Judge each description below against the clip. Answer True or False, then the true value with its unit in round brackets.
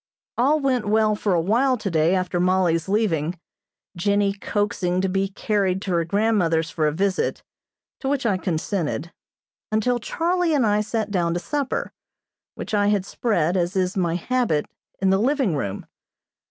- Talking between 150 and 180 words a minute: True (165 wpm)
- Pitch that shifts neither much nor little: True (4.0 semitones)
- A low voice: False (195 Hz)